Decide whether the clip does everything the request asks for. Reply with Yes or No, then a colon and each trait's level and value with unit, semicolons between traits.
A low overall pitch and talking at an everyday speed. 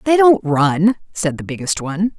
No: medium, 185 Hz; average, 190 wpm